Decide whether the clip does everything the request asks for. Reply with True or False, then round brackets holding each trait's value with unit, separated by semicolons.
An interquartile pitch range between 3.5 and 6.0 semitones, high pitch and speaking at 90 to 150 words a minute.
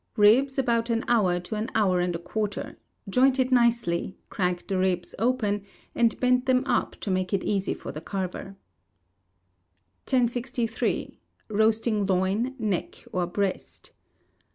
True (4.3 semitones; 215 Hz; 140 wpm)